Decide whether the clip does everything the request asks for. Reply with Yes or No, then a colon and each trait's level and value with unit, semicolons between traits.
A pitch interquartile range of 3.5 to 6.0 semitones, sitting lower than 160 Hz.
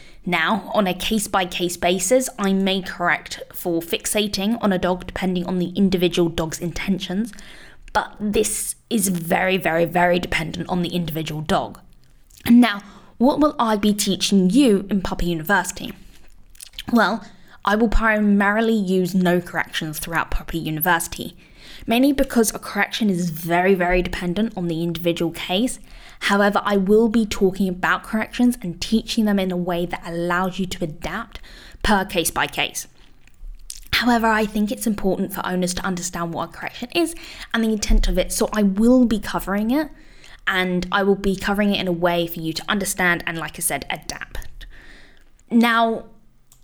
No: average, 3.8 semitones; high, 195 Hz